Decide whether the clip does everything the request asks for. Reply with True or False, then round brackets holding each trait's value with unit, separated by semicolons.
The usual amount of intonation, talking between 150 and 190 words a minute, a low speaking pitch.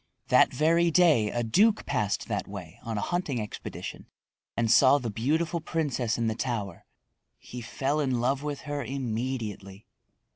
True (4.8 semitones; 155 wpm; 130 Hz)